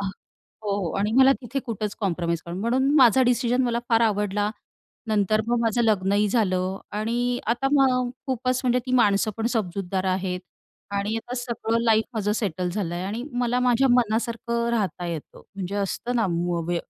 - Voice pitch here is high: Yes, high, 220 Hz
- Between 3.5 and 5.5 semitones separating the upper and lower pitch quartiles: Yes, average, 3.8 semitones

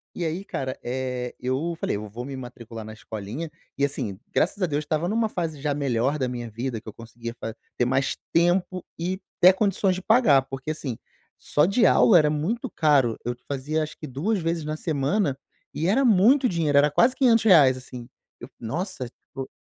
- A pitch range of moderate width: No, wide, 6.0 semitones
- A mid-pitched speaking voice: Yes, medium, 150 Hz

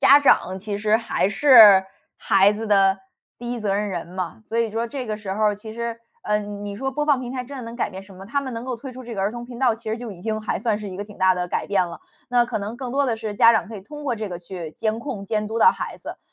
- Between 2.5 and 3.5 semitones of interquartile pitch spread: Yes, average, 3.2 semitones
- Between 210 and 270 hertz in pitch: Yes, high, 220 Hz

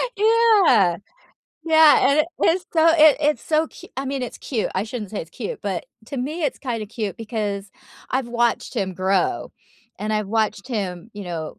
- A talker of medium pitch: No, high, 230 Hz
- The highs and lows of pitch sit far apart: Yes, wide, 6.9 semitones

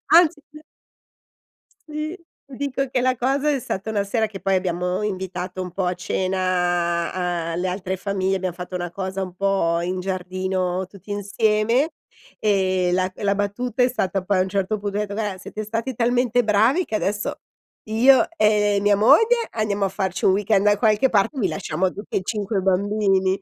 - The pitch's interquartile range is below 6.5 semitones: Yes, average, 2.7 semitones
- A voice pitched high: Yes, high, 200 Hz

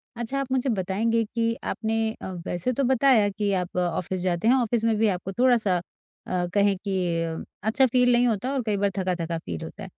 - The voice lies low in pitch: No, high, 215 Hz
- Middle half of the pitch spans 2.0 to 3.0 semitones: No, average, 4.7 semitones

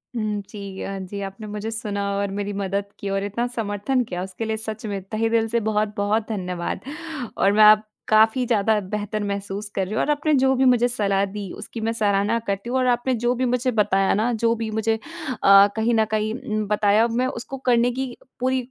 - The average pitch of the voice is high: Yes, high, 215 Hz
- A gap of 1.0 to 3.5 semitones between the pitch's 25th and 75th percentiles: Yes, narrow, 2.5 semitones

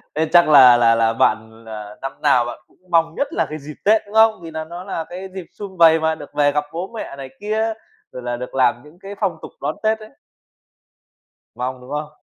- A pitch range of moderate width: No, wide, 6.7 semitones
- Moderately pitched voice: Yes, medium, 155 Hz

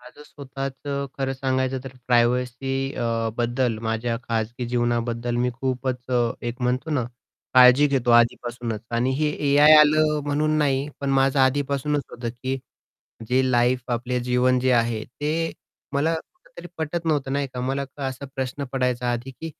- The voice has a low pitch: Yes, low, 130 Hz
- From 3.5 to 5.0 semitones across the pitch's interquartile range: No, narrow, 2.5 semitones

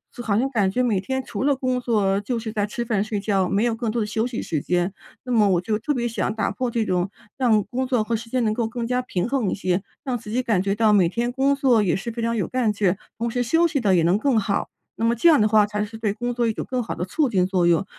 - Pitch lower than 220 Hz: No, high, 225 Hz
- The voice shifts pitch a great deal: No, average, 3.4 semitones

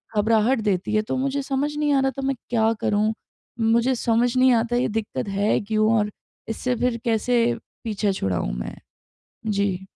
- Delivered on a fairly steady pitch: No, average, 3.4 semitones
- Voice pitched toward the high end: Yes, high, 225 Hz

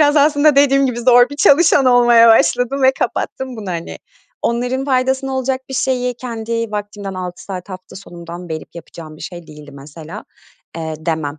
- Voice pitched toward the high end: Yes, high, 230 Hz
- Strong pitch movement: Yes, wide, 7.1 semitones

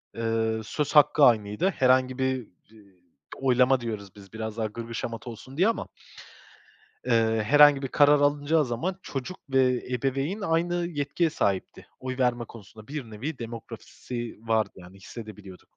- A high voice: No, low, 125 Hz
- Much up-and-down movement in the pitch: No, average, 4.3 semitones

